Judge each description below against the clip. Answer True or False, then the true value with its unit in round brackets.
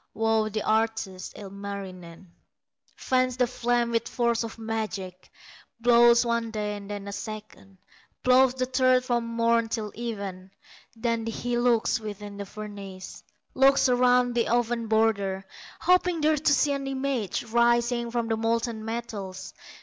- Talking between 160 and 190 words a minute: False (140 wpm)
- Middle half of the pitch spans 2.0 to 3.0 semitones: True (2.7 semitones)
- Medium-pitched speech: False (230 Hz)